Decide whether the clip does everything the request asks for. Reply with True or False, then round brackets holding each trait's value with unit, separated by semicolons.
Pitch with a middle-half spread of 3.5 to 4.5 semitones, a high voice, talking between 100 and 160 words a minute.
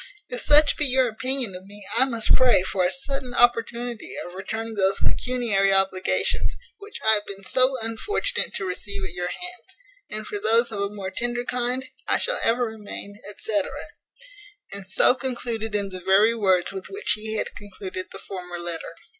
False (4.1 semitones; 215 Hz; 180 wpm)